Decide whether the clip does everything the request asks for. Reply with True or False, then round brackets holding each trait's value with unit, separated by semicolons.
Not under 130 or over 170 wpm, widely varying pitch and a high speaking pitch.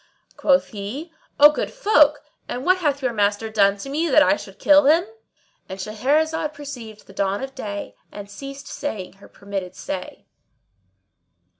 True (160 wpm; 6.6 semitones; 260 Hz)